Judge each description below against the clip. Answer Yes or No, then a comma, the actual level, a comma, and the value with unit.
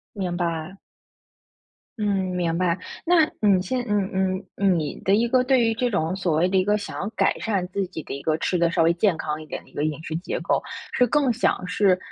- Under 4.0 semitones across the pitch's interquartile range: Yes, average, 3.6 semitones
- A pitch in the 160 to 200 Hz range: Yes, medium, 185 Hz